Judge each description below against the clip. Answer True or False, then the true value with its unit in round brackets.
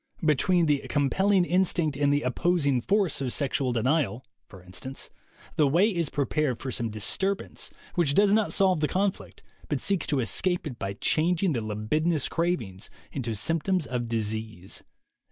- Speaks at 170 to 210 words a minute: False (155 wpm)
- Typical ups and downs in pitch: False (6.7 semitones)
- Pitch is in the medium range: True (145 Hz)